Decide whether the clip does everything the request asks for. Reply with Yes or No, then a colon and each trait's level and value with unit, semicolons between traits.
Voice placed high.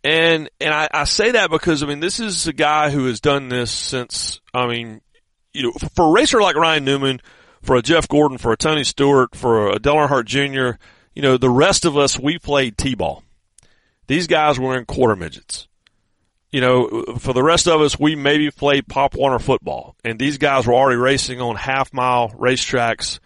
No: low, 135 Hz